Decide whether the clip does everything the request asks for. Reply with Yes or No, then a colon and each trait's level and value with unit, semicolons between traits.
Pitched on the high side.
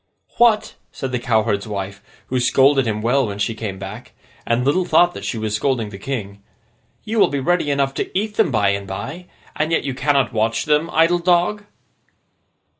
No: low, 130 Hz